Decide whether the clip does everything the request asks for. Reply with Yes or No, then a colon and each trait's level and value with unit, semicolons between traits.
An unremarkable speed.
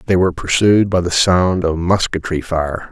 Yes: average, 185 wpm